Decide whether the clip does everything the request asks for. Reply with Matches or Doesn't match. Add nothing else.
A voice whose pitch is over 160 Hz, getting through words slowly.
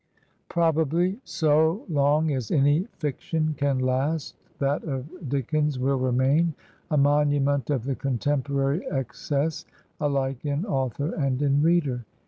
Doesn't match